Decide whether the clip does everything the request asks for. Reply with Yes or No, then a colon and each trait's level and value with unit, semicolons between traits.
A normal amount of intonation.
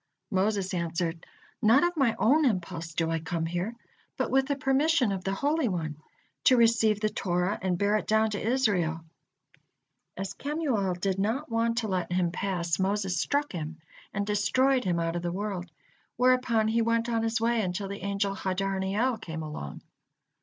Yes: average, 4.5 semitones